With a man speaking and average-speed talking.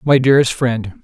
Yes: male; average, 175 wpm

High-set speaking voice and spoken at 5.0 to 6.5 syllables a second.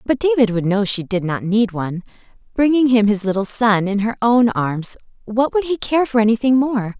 Yes: high, 225 Hz; 5.2 syllables/s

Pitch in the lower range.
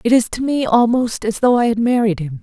No: high, 225 Hz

